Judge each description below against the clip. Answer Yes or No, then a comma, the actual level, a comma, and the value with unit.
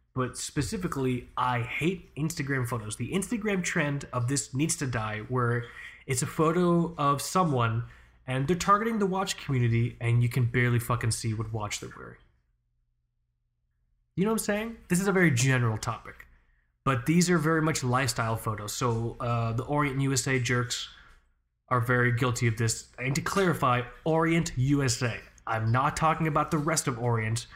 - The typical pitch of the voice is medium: No, low, 125 Hz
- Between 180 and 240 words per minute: No, average, 170 wpm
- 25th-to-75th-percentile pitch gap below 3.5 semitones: No, wide, 5.5 semitones